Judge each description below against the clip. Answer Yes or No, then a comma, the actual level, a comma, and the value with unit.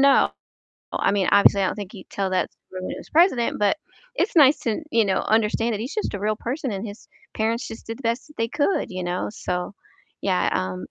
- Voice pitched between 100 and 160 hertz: No, high, 215 Hz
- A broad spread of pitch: No, average, 3.8 semitones